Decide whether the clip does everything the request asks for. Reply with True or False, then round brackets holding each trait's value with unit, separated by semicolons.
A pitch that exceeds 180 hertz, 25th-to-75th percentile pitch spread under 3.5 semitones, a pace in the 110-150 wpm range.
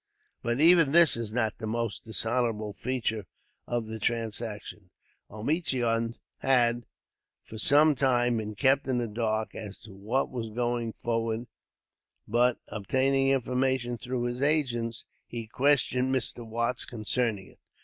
False (120 Hz; 2.6 semitones; 135 wpm)